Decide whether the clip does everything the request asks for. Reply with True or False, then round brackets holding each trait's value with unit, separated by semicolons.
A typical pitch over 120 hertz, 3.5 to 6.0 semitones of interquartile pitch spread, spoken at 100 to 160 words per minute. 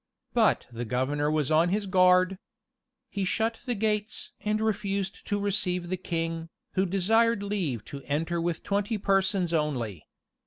True (185 Hz; 3.9 semitones; 150 wpm)